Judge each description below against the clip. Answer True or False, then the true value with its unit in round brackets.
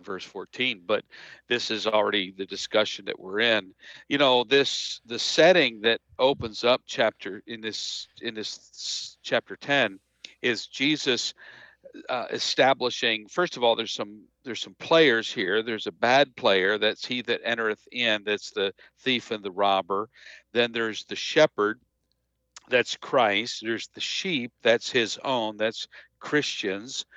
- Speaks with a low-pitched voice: True (115 Hz)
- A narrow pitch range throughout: False (3.6 semitones)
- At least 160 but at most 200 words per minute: False (150 wpm)